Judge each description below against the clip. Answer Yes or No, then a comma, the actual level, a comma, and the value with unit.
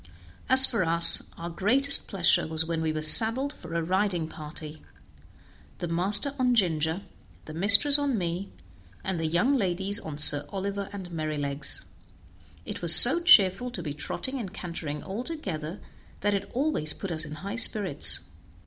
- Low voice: No, medium, 185 Hz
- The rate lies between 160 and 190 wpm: Yes, average, 165 wpm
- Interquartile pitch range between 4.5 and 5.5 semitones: Yes, average, 5.1 semitones